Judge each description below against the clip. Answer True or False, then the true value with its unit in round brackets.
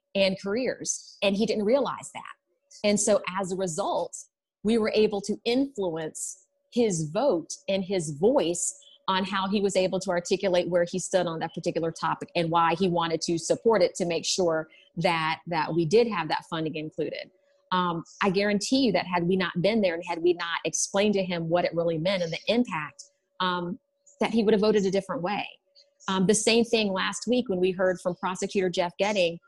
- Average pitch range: True (3.5 semitones)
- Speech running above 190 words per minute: True (205 wpm)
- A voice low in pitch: False (190 Hz)